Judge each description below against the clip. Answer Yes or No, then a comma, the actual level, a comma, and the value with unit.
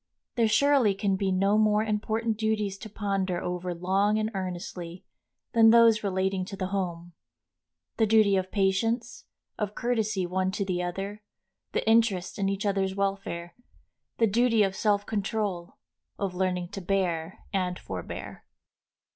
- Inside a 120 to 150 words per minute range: Yes, average, 145 wpm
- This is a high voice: Yes, high, 195 Hz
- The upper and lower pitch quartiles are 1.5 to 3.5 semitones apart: Yes, narrow, 2.6 semitones